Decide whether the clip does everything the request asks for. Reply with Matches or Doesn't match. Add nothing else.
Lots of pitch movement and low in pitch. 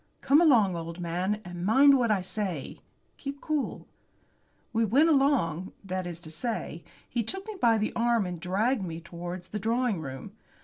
Doesn't match